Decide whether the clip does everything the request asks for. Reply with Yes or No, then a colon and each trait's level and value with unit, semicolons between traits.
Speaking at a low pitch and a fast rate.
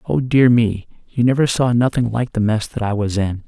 Yes: low, 115 Hz; fast, 240 wpm